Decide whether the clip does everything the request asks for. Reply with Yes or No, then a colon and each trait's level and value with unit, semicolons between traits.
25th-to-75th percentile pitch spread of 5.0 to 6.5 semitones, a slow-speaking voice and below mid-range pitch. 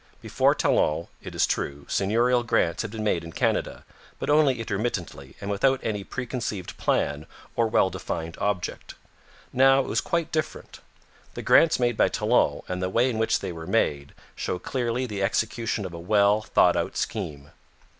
No: average, 5.3 semitones; average, 175 wpm; low, 105 Hz